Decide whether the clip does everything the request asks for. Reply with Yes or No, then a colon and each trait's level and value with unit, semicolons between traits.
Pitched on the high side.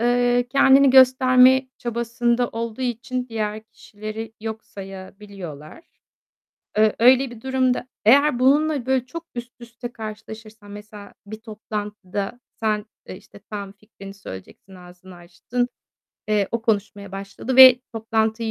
Yes: high, 225 Hz